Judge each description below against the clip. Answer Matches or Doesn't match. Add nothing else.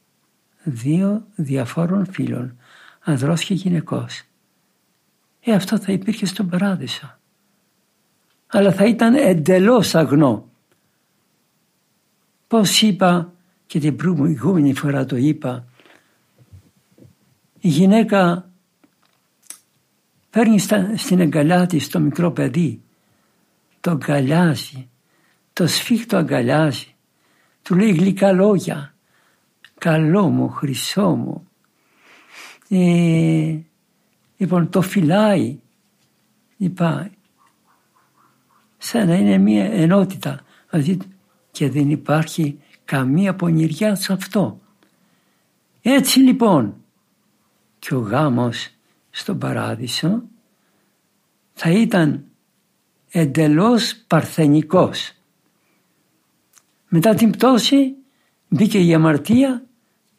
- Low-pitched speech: Doesn't match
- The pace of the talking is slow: Matches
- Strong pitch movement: Doesn't match